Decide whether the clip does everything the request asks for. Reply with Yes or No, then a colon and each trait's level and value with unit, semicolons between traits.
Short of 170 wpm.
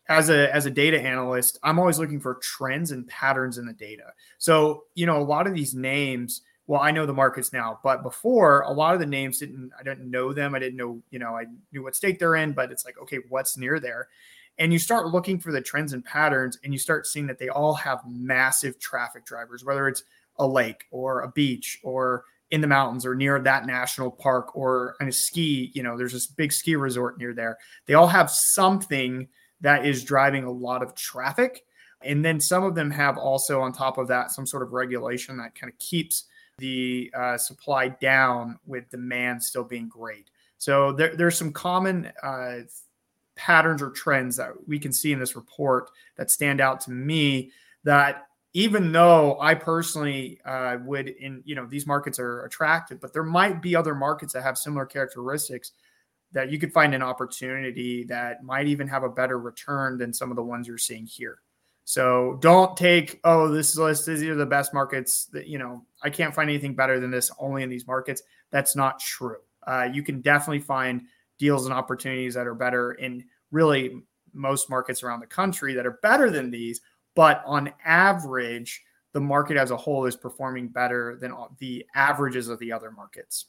No: fast, 205 wpm